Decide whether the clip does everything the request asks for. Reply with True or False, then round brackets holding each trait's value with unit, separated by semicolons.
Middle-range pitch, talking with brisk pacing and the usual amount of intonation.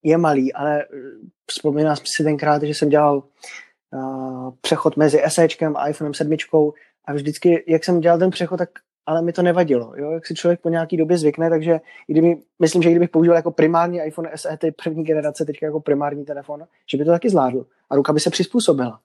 False (155 Hz; 200 wpm; 2.2 semitones)